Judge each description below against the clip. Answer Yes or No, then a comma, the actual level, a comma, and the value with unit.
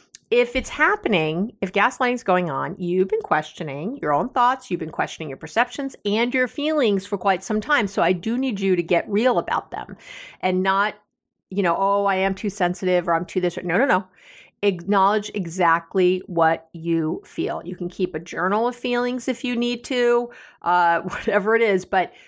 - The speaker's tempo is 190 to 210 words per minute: Yes, average, 200 wpm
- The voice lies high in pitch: Yes, high, 195 Hz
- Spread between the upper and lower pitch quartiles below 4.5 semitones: No, average, 5.3 semitones